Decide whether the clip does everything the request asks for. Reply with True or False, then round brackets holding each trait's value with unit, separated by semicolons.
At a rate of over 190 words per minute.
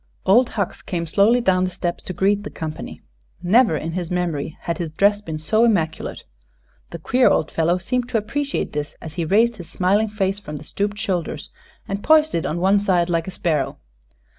True (200 wpm)